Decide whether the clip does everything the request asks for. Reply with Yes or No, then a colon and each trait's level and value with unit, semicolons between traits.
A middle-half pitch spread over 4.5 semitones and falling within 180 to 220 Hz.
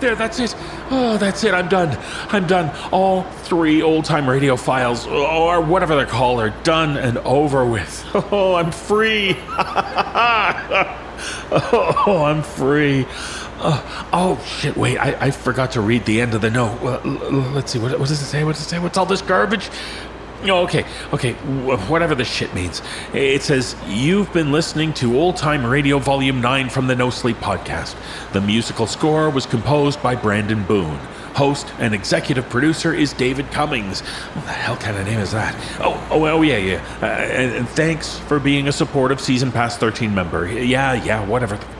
No: average, 5.0 semitones; medium, 140 Hz